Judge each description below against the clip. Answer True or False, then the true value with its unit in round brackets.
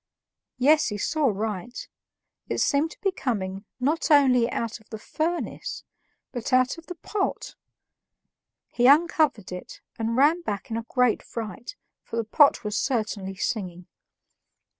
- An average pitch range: False (5.7 semitones)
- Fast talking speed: False (145 wpm)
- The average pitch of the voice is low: False (245 Hz)